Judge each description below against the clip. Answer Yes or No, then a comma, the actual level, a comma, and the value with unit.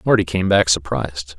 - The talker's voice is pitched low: Yes, very low, 85 Hz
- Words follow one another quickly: No, average, 175 wpm